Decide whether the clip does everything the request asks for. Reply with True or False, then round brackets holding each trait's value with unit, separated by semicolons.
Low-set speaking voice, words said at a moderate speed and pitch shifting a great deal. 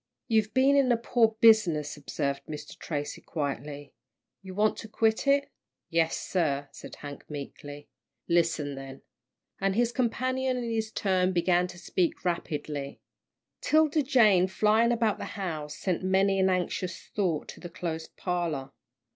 False (185 Hz; 150 wpm; 6.6 semitones)